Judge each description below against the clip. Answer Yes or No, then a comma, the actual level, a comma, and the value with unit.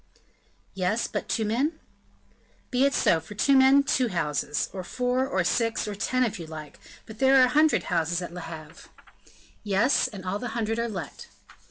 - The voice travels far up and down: Yes, wide, 6.1 semitones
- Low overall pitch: No, high, 220 Hz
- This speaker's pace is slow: No, average, 190 wpm